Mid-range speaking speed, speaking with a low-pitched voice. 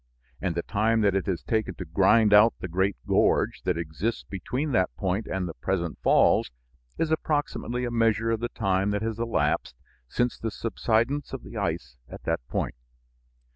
Yes: average, 180 wpm; low, 105 Hz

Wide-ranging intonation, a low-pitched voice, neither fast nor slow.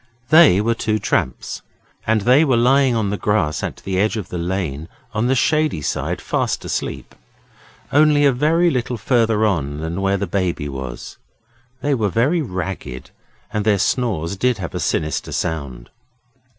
Yes: wide, 6.8 semitones; low, 105 Hz; average, 165 wpm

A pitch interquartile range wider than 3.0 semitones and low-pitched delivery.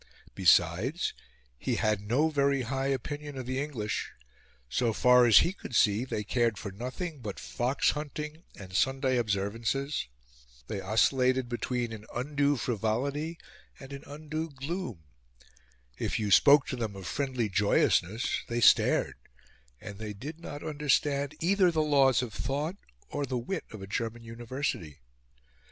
Yes: average, 4.8 semitones; low, 130 Hz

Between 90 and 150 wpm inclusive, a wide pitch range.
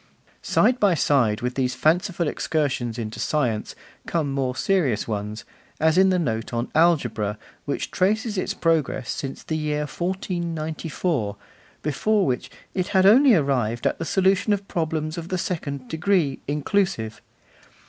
Yes: average, 145 wpm; wide, 6.3 semitones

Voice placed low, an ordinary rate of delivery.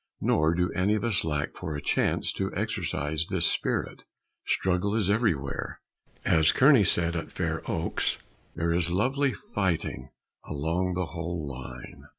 Yes: very low, 85 Hz; average, 150 wpm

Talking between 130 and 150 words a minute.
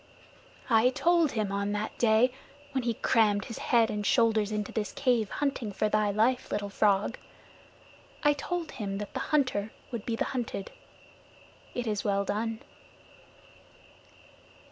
Yes: average, 145 wpm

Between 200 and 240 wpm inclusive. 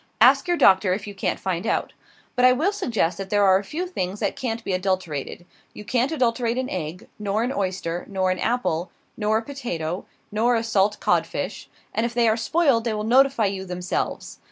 Yes: fast, 205 wpm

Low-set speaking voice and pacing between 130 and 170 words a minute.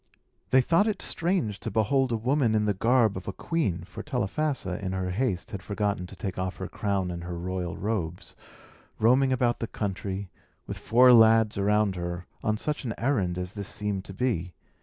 No: low, 105 Hz; average, 195 wpm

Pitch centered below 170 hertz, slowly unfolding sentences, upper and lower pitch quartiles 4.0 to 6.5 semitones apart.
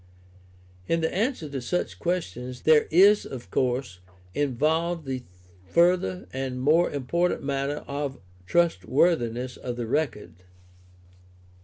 Yes: medium, 140 Hz; slow, 120 wpm; average, 5.2 semitones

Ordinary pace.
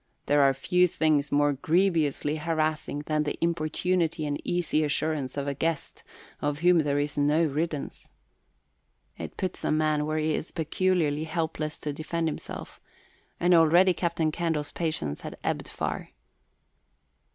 Yes: average, 145 wpm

